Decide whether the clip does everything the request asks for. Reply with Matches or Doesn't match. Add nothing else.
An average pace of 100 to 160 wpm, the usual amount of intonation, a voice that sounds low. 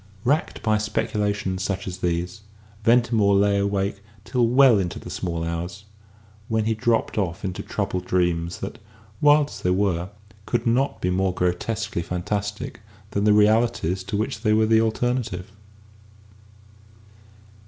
Matches